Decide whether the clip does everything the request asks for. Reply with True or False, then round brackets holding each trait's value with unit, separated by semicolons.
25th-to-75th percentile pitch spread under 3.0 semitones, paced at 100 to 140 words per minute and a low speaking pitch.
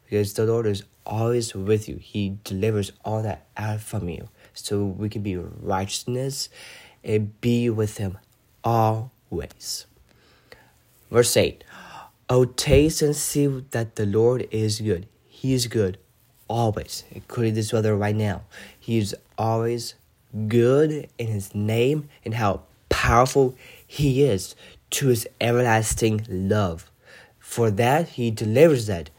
True (2.6 semitones; 135 wpm; 110 Hz)